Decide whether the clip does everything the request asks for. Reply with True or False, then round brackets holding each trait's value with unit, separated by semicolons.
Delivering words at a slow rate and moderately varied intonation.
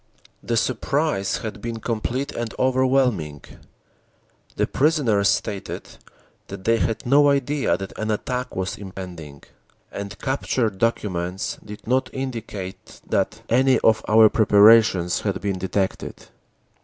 True (120 wpm; 4.9 semitones)